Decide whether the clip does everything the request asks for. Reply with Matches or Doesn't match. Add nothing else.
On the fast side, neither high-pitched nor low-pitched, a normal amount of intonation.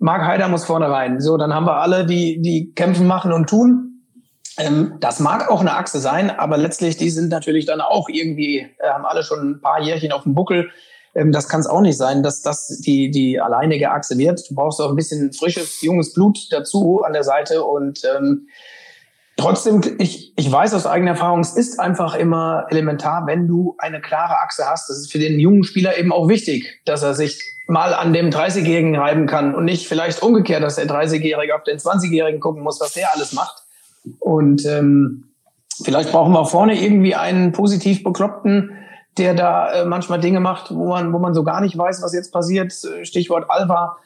Matches